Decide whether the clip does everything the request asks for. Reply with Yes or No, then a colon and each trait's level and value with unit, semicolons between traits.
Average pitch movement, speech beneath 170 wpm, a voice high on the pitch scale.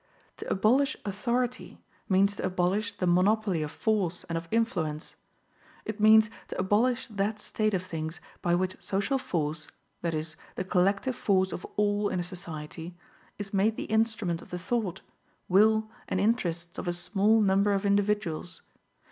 Yes: average, 3.6 semitones; average, 160 wpm; high, 195 Hz